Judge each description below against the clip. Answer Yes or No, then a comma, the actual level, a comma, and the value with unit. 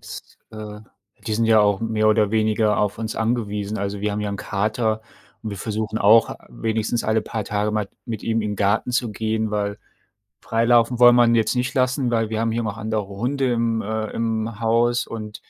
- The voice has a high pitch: No, low, 110 Hz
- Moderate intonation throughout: No, narrow, 1.5 semitones